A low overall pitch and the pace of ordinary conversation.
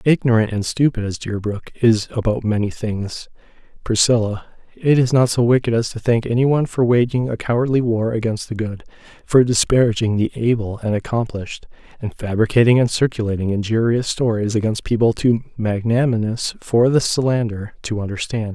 Yes: low, 115 Hz; average, 160 wpm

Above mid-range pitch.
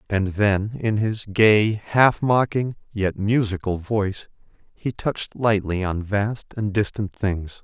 No: low, 105 Hz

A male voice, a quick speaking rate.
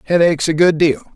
Yes: male; fast, 260 wpm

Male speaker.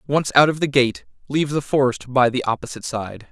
Yes: male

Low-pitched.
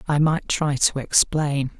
No: medium, 145 Hz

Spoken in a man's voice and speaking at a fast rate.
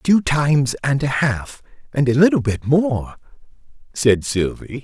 No: male; average, 150 wpm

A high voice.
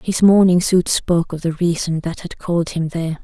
No: medium, 170 Hz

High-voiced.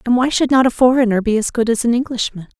Yes: high, 240 Hz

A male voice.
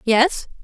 No: female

